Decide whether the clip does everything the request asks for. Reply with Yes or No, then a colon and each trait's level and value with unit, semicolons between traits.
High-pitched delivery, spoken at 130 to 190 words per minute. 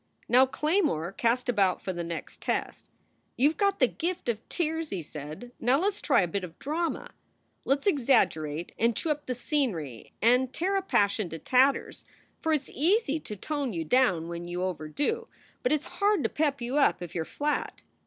No: very high, 255 Hz; fast, 205 wpm